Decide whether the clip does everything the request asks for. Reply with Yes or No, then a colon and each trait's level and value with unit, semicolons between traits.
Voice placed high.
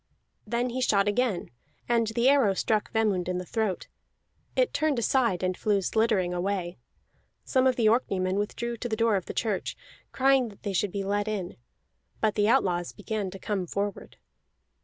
Yes: high, 210 Hz